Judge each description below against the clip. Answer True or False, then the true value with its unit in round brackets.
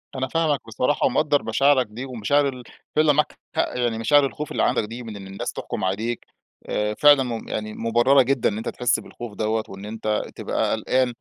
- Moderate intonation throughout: True (4.1 semitones)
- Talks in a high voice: False (120 Hz)